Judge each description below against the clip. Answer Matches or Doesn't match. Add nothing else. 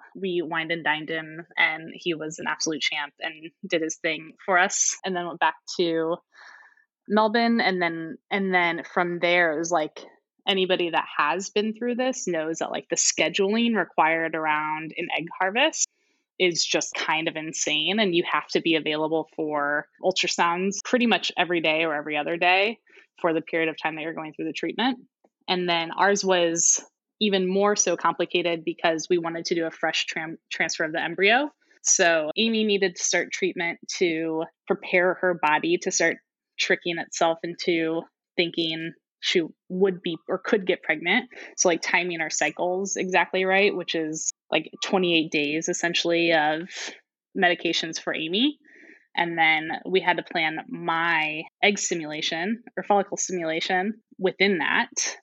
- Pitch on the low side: Doesn't match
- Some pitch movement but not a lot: Matches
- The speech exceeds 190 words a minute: Doesn't match